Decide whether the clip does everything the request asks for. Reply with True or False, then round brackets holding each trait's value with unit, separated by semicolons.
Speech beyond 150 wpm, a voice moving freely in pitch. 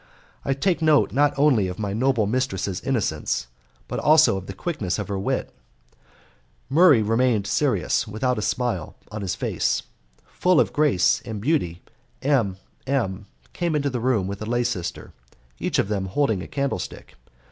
True (165 wpm; 6.0 semitones)